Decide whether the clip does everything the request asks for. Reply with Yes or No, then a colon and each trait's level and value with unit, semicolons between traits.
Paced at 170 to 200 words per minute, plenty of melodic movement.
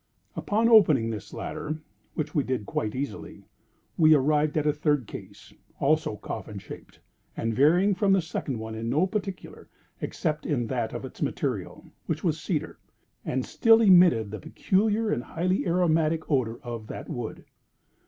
No: average, 160 wpm; wide, 7.0 semitones